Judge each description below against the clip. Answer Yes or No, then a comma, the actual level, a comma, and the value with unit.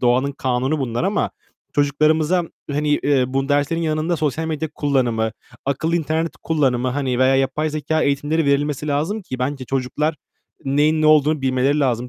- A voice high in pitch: No, medium, 145 Hz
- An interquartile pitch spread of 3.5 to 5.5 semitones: No, average, 2.8 semitones